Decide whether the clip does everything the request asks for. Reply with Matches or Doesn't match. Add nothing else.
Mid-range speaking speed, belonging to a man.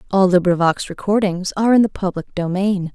Doesn't match